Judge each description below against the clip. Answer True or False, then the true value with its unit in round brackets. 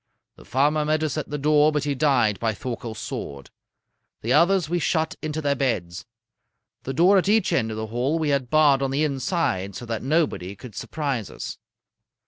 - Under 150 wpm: False (195 wpm)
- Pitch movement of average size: True (4.9 semitones)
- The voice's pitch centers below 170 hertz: True (140 Hz)